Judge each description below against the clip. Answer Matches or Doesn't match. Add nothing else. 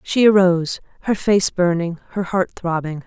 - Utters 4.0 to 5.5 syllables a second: Matches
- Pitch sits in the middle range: Matches